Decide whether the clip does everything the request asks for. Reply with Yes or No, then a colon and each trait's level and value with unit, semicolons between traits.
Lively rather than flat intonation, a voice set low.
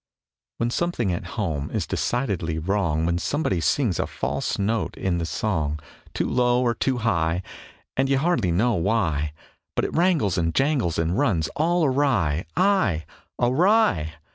Yes: wide, 8.3 semitones; low, 105 Hz